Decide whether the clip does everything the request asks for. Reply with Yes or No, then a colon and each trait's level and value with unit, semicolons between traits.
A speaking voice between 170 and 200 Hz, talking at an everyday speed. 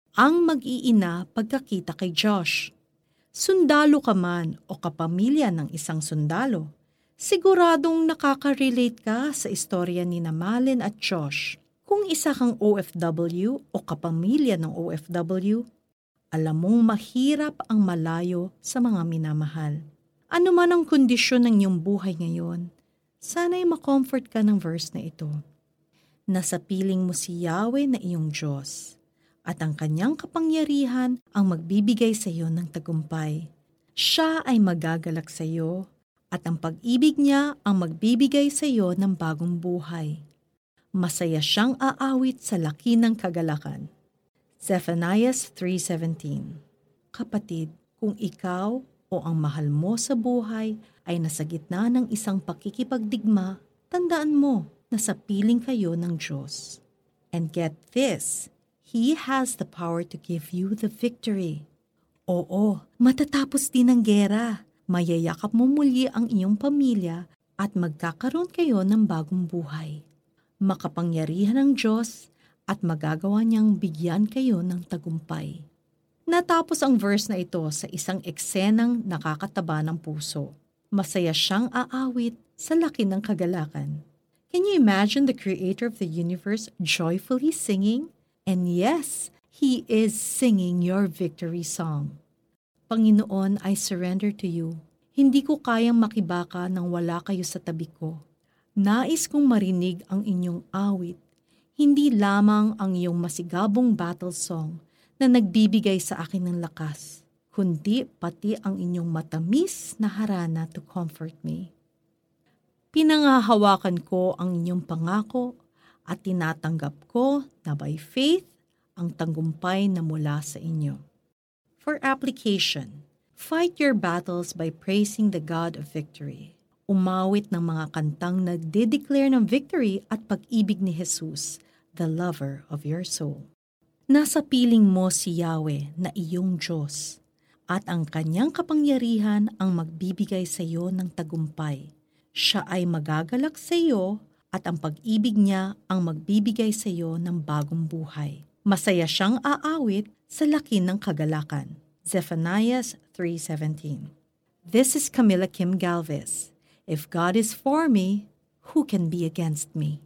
Yes: medium, 185 Hz; average, 130 wpm